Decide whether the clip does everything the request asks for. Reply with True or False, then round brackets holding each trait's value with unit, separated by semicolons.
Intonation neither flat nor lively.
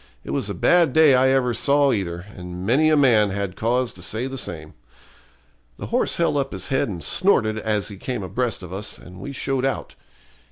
False (5.7 semitones)